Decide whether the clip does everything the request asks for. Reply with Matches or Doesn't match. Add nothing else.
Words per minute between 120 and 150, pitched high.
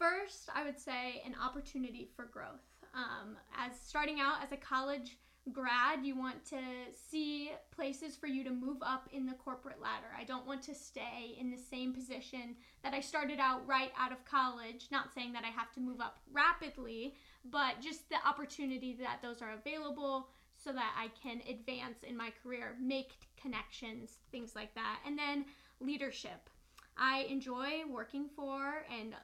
Doesn't match